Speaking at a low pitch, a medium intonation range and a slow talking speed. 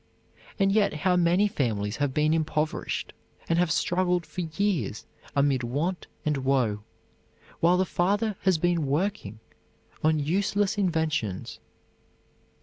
No: medium, 165 Hz; average, 4.8 semitones; slow, 125 wpm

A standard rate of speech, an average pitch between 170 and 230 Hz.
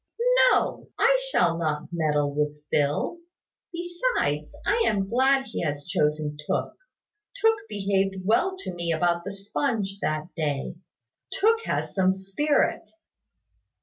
No: slow, 125 wpm; high, 190 Hz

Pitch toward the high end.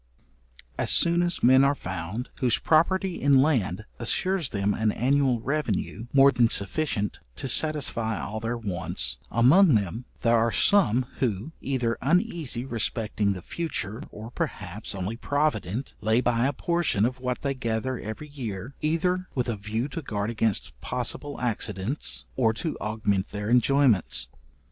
No: low, 120 Hz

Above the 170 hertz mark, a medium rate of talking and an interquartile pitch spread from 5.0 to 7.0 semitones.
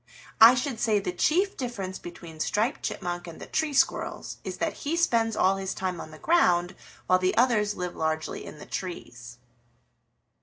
Yes: high, 190 Hz; average, 180 wpm; wide, 5.5 semitones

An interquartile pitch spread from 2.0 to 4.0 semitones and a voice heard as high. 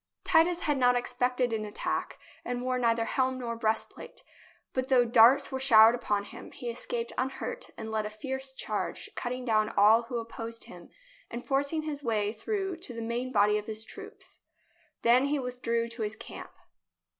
Yes: average, 2.8 semitones; high, 245 Hz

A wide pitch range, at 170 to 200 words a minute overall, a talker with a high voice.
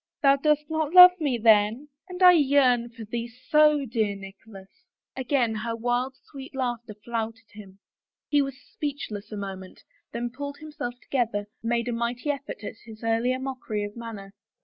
No: average, 4.2 semitones; average, 175 wpm; high, 240 Hz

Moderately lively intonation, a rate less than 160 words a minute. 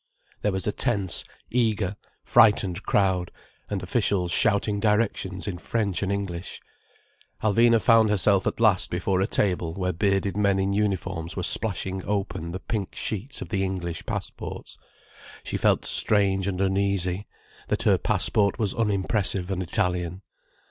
No: narrow, 2.2 semitones; average, 150 wpm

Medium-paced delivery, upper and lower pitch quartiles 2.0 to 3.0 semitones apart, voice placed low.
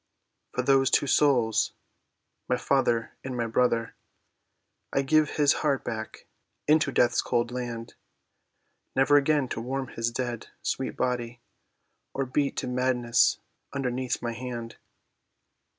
No: slow, 120 wpm; narrow, 2.5 semitones; low, 125 Hz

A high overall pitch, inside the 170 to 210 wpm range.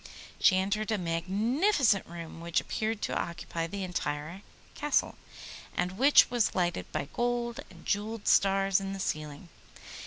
No: high, 195 Hz; average, 145 wpm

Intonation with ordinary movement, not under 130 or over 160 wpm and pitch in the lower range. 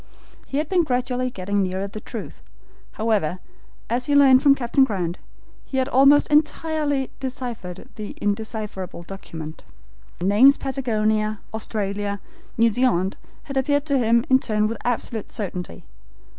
No: average, 4.8 semitones; average, 140 wpm; high, 230 Hz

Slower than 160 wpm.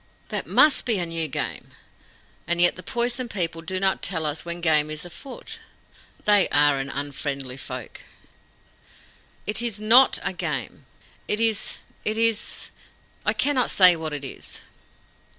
Yes: average, 150 wpm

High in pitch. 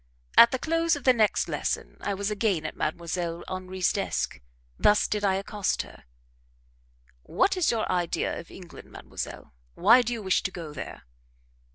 Yes: high, 200 Hz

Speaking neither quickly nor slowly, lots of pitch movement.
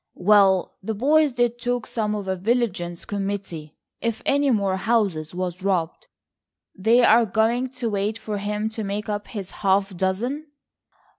No: average, 155 wpm; average, 3.6 semitones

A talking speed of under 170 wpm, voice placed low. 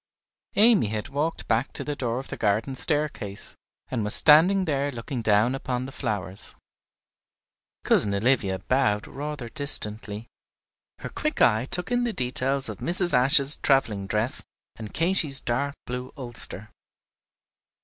Yes: average, 140 wpm; low, 130 Hz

